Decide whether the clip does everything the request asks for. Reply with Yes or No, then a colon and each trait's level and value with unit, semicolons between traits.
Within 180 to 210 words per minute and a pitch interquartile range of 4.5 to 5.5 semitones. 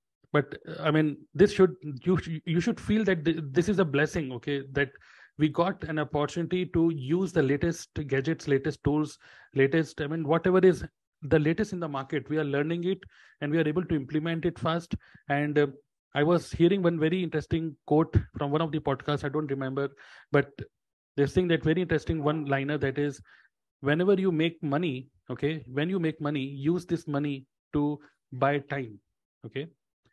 No: average, 185 wpm; average, 2.9 semitones